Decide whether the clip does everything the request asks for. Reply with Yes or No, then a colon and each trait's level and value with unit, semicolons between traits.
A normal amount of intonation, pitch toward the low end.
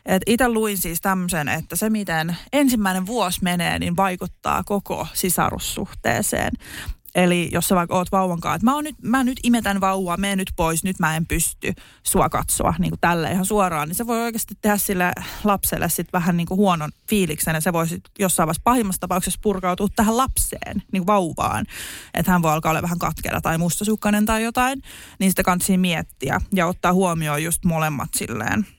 No: average, 3.3 semitones; medium, 185 Hz